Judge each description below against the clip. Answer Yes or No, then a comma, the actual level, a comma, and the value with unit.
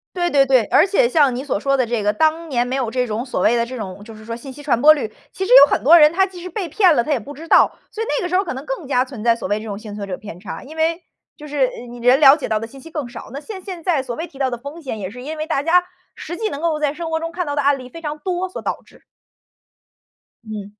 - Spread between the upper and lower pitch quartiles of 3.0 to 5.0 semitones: No, wide, 5.5 semitones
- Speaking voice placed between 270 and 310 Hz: Yes, very high, 280 Hz